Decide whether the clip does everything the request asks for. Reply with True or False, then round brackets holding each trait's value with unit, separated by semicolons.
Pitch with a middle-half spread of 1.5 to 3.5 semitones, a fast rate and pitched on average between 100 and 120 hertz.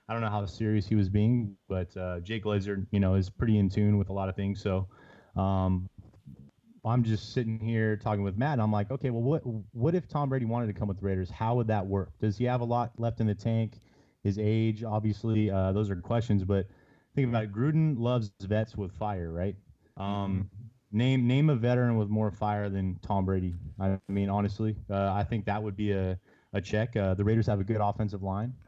True (2.6 semitones; 225 wpm; 105 Hz)